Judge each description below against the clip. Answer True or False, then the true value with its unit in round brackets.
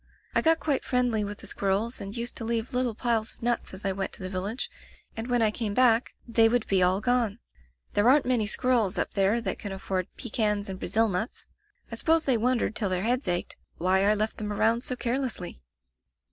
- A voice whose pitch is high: True (225 Hz)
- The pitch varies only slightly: False (3.6 semitones)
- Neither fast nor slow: False (225 wpm)